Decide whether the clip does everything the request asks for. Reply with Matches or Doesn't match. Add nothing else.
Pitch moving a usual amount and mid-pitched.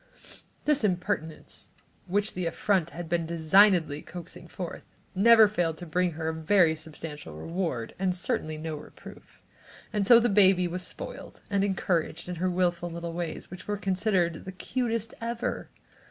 Matches